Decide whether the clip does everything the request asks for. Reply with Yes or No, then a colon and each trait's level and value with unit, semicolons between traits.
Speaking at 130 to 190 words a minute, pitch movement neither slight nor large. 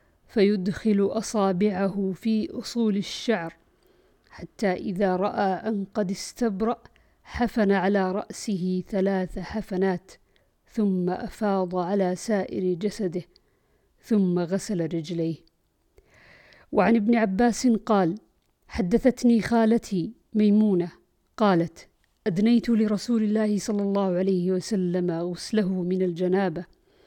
No: average, 95 wpm; average, 3.0 semitones